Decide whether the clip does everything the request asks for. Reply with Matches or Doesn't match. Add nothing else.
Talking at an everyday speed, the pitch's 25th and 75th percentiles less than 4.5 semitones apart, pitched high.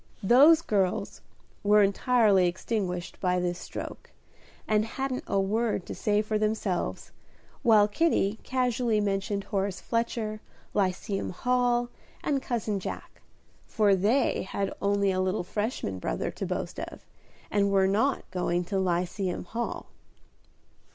Doesn't match